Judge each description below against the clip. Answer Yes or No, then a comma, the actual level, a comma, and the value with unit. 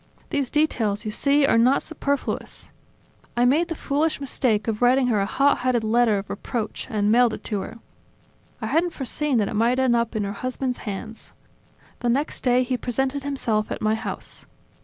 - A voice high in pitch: Yes, high, 245 Hz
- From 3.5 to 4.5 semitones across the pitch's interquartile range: Yes, average, 4.1 semitones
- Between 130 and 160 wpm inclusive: No, average, 190 wpm